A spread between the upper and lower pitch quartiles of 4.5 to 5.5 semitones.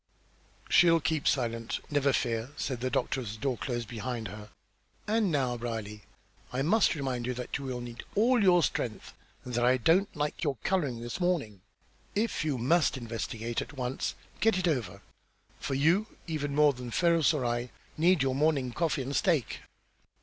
Yes: average, 5.2 semitones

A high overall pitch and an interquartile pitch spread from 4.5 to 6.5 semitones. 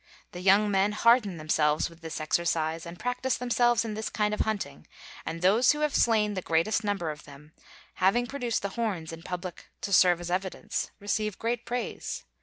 Yes: high, 200 Hz; average, 5.1 semitones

